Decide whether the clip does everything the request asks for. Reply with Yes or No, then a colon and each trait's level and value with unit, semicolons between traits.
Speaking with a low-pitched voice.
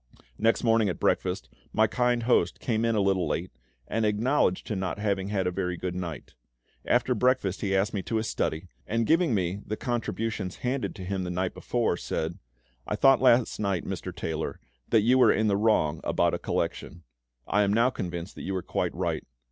Yes: low, 105 Hz